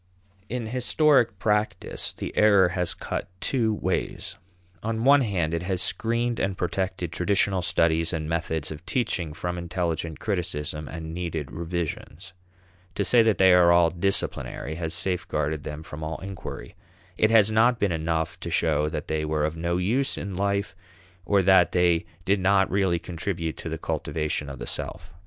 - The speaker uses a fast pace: No, average, 165 wpm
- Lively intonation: No, average, 3.7 semitones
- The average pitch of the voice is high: No, very low, 90 Hz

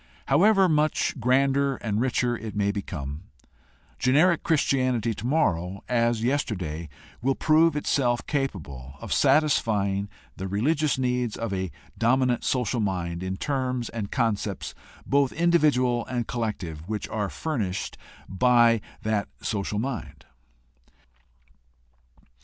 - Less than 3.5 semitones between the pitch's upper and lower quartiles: No, average, 5.3 semitones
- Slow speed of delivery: Yes, slow, 110 wpm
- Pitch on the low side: Yes, low, 120 Hz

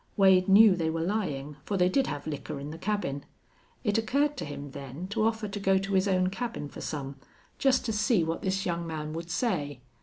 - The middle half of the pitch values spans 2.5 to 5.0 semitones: No, wide, 5.6 semitones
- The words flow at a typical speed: No, fast, 220 wpm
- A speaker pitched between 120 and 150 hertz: No, medium, 185 Hz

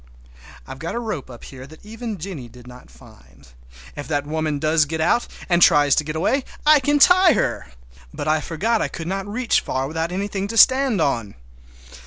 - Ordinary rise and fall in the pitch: No, wide, 7.3 semitones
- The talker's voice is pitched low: No, medium, 160 Hz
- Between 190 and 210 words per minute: Yes, average, 200 wpm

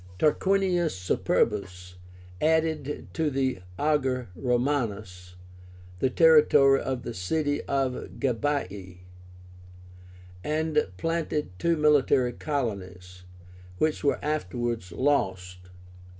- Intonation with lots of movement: Yes, wide, 7.4 semitones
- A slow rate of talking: Yes, slow, 85 wpm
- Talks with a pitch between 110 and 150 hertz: Yes, low, 135 Hz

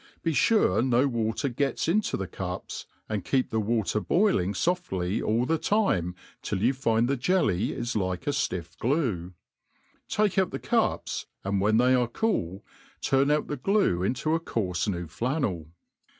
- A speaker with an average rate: Yes, average, 165 wpm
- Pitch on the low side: Yes, low, 120 Hz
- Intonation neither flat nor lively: No, wide, 7.5 semitones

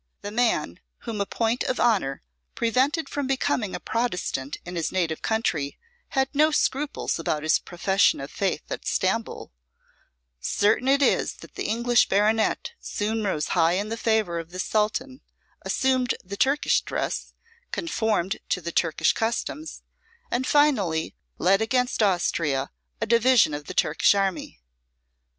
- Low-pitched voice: No, high, 215 Hz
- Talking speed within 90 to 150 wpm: Yes, average, 145 wpm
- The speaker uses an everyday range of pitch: No, wide, 5.8 semitones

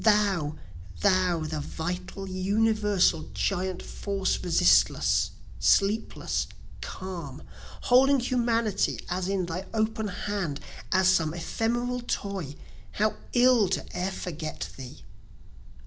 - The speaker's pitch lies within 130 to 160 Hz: No, high, 190 Hz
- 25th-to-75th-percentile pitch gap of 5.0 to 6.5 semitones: No, average, 3.8 semitones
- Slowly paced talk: Yes, slow, 100 wpm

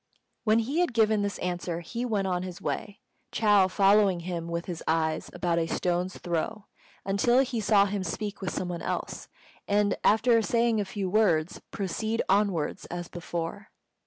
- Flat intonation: No, average, 3.6 semitones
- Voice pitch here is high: Yes, high, 195 Hz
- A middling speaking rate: Yes, average, 170 wpm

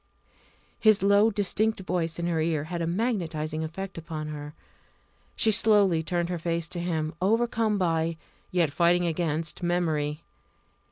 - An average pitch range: Yes, average, 3.3 semitones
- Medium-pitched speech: Yes, medium, 170 Hz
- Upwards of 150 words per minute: No, average, 145 wpm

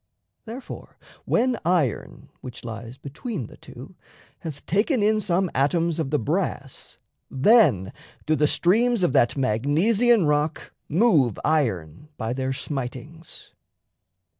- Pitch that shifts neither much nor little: No, wide, 6.9 semitones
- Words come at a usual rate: No, slow, 120 wpm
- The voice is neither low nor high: Yes, medium, 155 Hz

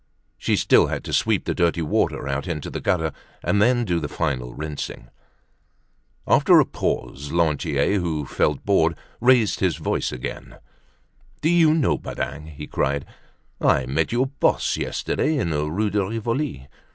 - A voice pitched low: Yes, very low, 85 Hz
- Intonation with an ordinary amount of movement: No, wide, 6.9 semitones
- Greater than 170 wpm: No, average, 160 wpm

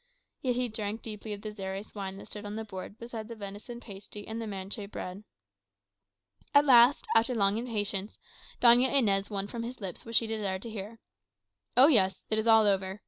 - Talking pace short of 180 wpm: No, average, 195 wpm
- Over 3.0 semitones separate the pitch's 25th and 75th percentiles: No, average, 2.7 semitones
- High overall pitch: Yes, high, 215 Hz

